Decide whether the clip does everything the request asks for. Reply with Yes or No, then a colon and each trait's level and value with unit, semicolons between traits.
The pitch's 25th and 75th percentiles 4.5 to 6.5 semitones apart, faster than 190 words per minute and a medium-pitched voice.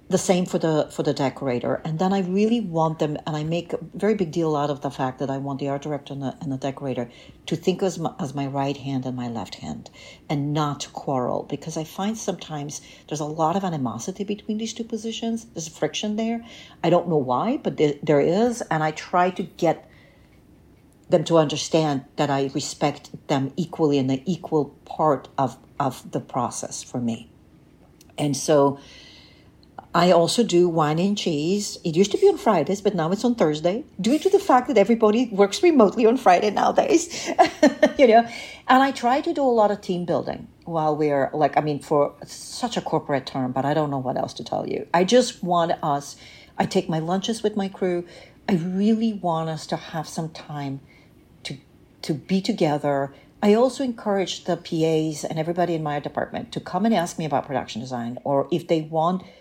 Yes: wide, 5.5 semitones; fast, 205 wpm; medium, 165 Hz